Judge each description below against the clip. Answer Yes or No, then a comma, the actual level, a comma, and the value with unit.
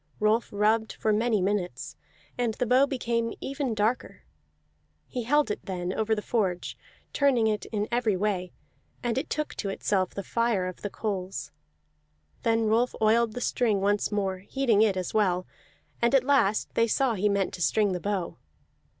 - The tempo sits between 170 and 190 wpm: Yes, average, 175 wpm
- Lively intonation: No, average, 3.0 semitones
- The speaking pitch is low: No, high, 215 Hz